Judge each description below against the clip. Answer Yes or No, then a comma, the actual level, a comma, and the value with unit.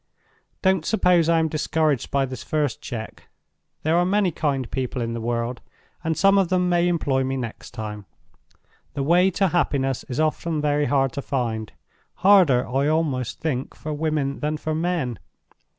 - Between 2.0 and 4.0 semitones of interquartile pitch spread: No, average, 4.5 semitones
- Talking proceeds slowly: No, average, 170 wpm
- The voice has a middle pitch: Yes, medium, 150 Hz